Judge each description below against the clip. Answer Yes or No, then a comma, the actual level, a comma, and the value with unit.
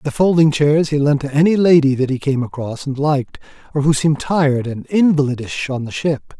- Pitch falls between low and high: Yes, medium, 145 Hz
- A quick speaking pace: Yes, fast, 215 wpm